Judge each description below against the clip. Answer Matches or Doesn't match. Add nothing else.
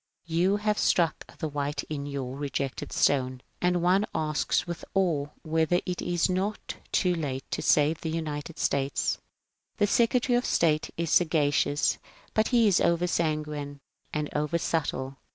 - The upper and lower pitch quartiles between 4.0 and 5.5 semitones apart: Doesn't match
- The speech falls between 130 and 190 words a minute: Matches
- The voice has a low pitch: Doesn't match